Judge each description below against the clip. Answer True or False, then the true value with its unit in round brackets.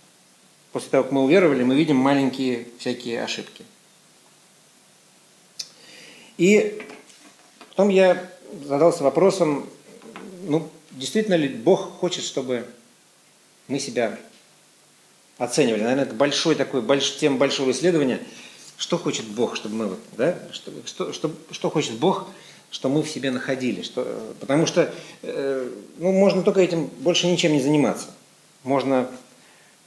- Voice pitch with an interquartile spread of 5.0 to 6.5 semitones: True (5.5 semitones)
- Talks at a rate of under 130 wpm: True (120 wpm)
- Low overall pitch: False (155 Hz)